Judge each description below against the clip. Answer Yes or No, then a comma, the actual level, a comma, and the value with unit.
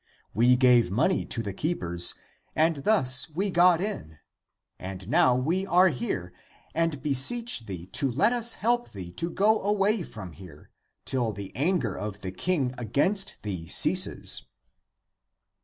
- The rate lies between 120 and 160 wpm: Yes, average, 145 wpm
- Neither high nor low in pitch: No, low, 130 Hz